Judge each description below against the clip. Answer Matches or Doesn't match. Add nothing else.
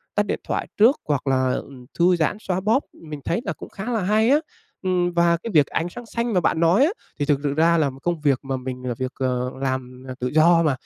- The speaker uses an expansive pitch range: Matches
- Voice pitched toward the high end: Doesn't match